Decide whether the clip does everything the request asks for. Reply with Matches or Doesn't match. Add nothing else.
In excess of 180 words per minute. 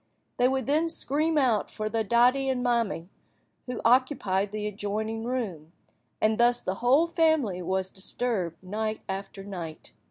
Doesn't match